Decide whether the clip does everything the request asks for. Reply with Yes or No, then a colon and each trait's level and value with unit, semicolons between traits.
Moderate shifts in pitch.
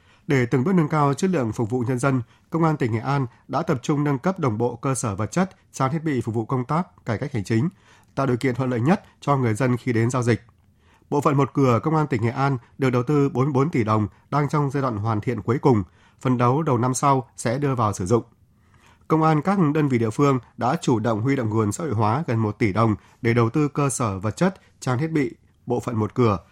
Yes: average, 4.0 semitones